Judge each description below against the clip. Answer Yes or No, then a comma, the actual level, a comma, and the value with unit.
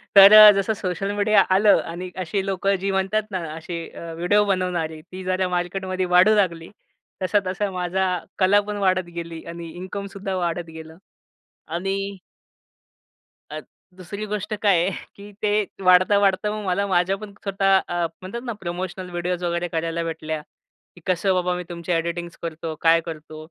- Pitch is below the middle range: No, medium, 185 Hz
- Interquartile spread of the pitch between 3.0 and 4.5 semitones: No, narrow, 2.5 semitones